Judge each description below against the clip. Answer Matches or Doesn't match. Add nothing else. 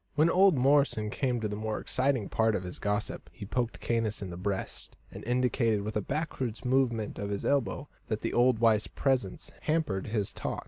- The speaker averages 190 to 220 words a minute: Matches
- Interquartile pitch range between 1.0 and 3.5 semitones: Doesn't match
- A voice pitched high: Doesn't match